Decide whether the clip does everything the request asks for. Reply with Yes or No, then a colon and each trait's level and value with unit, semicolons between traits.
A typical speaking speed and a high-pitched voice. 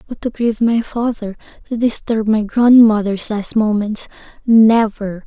No: slow, 115 wpm; high, 220 Hz